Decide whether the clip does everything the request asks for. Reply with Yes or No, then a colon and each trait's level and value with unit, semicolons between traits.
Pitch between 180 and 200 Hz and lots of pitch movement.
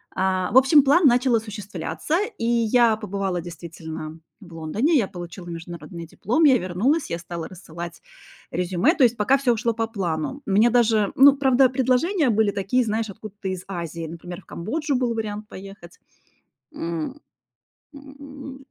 No: high, 215 Hz; wide, 6.7 semitones